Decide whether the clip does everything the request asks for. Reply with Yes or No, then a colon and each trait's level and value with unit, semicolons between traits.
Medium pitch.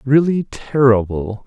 No: low, 125 Hz